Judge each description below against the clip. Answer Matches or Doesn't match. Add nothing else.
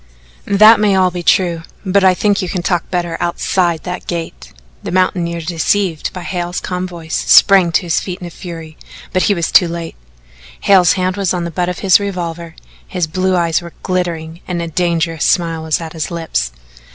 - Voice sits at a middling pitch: Matches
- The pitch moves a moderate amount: Doesn't match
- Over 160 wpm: Matches